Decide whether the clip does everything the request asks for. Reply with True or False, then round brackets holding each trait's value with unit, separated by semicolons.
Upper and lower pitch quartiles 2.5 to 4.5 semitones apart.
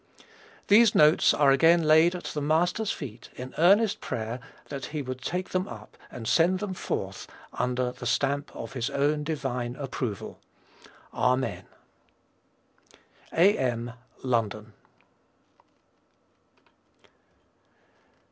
False (5.2 semitones)